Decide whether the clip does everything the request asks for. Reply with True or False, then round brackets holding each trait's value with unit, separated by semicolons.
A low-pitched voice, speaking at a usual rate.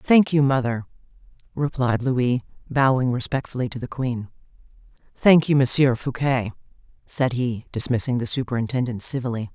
False (125 Hz; 125 wpm)